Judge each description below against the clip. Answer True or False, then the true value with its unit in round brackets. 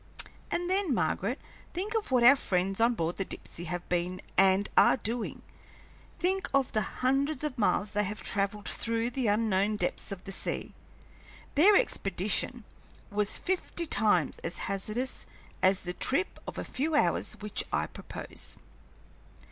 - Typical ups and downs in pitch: False (5.9 semitones)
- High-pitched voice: True (215 Hz)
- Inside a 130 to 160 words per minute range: True (155 wpm)